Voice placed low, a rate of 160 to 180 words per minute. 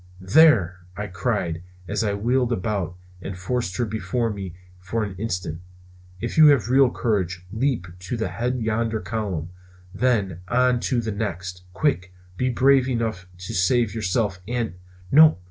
Yes: low, 110 Hz; average, 165 wpm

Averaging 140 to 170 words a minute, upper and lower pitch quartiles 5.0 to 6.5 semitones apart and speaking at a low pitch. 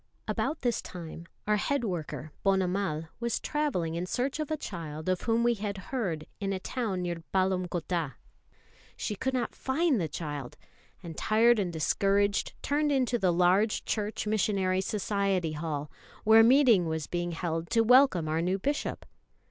No: average, 165 wpm; wide, 5.4 semitones; high, 195 Hz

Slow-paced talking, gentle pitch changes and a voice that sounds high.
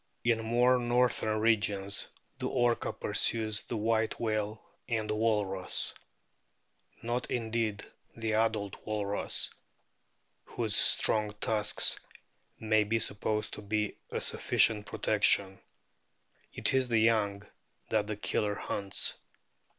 No: slow, 110 wpm; narrow, 1.6 semitones; low, 110 Hz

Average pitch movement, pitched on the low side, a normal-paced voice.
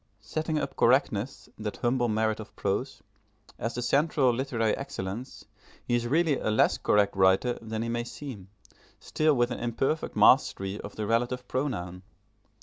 Yes: average, 3.8 semitones; low, 120 Hz; average, 155 wpm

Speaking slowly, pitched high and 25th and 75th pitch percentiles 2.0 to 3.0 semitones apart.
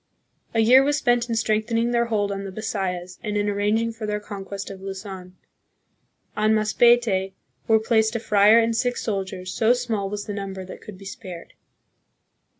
No: average, 175 wpm; high, 210 Hz; average, 2.7 semitones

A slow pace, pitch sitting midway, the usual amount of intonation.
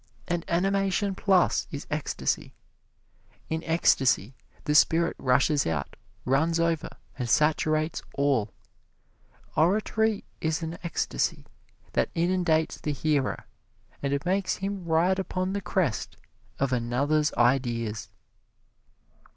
Yes: slow, 105 wpm; medium, 160 Hz; average, 4.6 semitones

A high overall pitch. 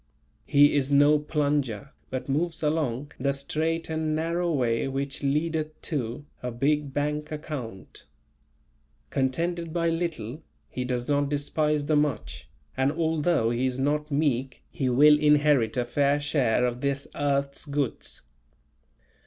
No: medium, 145 Hz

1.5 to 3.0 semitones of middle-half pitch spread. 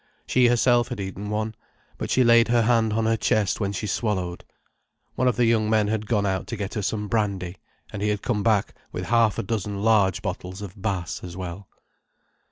Yes: narrow, 2.5 semitones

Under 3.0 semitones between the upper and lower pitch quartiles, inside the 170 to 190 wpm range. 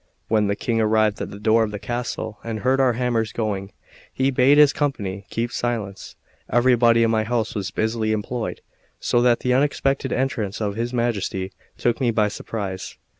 Yes: narrow, 2.6 semitones; average, 180 wpm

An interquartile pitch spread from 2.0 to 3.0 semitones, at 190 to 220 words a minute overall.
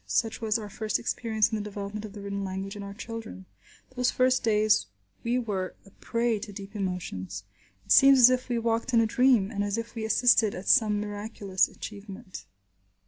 Yes: narrow, 2.5 semitones; average, 195 wpm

